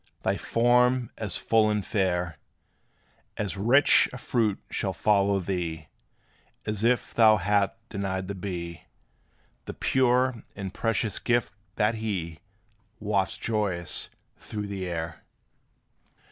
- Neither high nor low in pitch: No, low, 105 Hz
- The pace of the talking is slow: Yes, slow, 120 wpm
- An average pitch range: Yes, average, 3.3 semitones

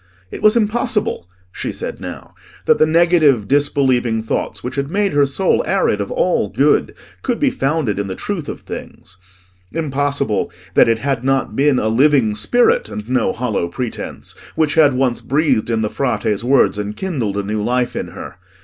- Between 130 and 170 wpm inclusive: No, average, 180 wpm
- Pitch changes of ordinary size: No, wide, 5.9 semitones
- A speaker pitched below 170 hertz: Yes, low, 135 Hz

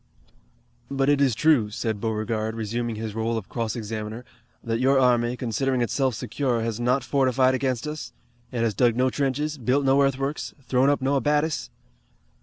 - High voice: No, low, 125 Hz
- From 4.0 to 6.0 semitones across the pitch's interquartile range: No, average, 3.1 semitones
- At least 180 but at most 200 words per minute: No, average, 170 wpm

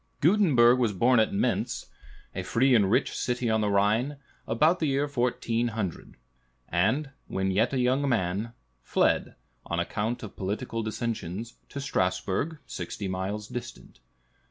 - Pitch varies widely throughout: No, average, 4.2 semitones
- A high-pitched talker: No, low, 115 Hz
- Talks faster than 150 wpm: No, average, 140 wpm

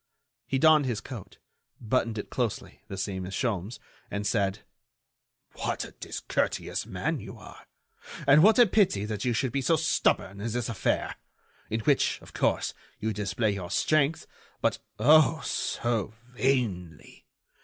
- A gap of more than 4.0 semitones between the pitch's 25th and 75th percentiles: Yes, average, 5.2 semitones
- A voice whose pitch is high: No, low, 115 Hz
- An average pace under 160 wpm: Yes, average, 150 wpm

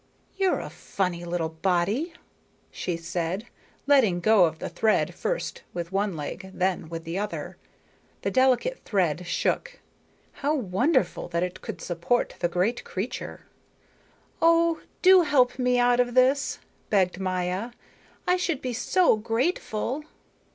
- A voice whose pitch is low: No, high, 215 Hz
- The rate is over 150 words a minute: No, slow, 135 wpm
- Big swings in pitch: Yes, wide, 6.8 semitones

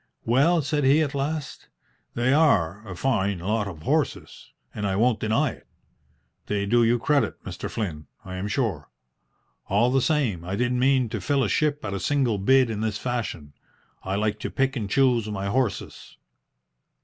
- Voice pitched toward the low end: Yes, low, 115 Hz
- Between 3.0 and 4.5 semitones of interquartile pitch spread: No, average, 5.1 semitones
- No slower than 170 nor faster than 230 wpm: Yes, average, 180 wpm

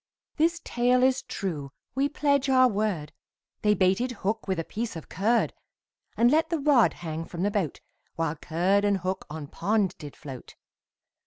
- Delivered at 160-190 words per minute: Yes, average, 170 wpm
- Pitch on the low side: No, high, 205 Hz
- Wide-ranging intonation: Yes, wide, 7.0 semitones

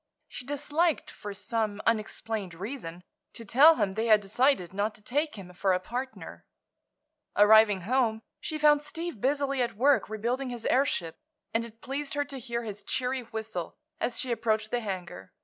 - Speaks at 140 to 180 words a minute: Yes, average, 170 wpm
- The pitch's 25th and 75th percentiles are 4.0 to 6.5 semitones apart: Yes, average, 4.6 semitones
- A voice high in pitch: Yes, high, 230 Hz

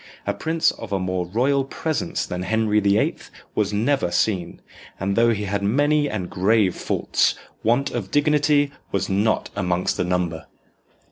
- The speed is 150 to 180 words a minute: Yes, average, 160 wpm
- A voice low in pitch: Yes, low, 105 Hz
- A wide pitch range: Yes, wide, 6.5 semitones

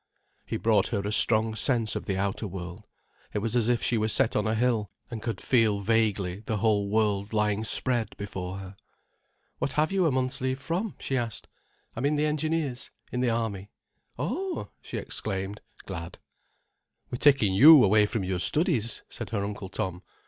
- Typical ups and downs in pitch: Yes, average, 4.3 semitones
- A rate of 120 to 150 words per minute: No, average, 180 wpm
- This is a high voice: No, low, 110 Hz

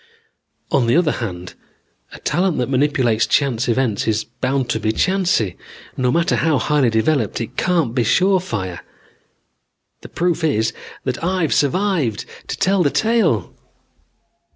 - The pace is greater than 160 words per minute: No, average, 140 wpm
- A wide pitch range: Yes, wide, 7.3 semitones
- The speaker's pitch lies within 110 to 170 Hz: Yes, low, 135 Hz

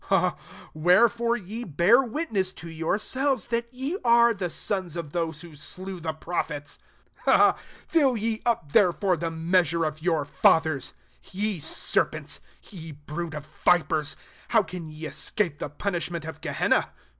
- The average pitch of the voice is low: No, medium, 175 Hz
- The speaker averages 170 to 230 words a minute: No, average, 155 wpm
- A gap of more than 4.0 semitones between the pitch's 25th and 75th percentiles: Yes, wide, 5.5 semitones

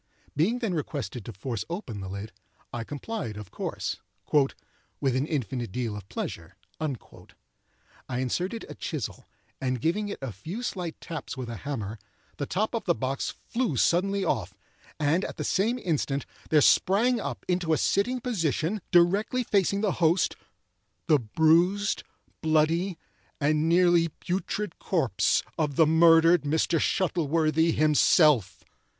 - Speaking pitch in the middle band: Yes, medium, 160 Hz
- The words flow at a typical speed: Yes, average, 145 wpm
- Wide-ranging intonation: Yes, wide, 5.8 semitones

